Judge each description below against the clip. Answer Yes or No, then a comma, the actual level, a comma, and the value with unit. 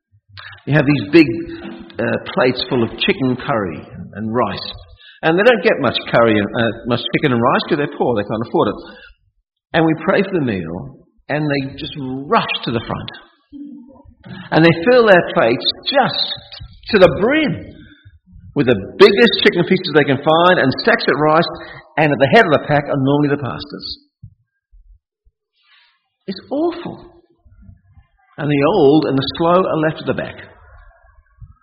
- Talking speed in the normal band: Yes, average, 170 wpm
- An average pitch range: No, wide, 6.6 semitones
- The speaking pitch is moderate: Yes, medium, 150 Hz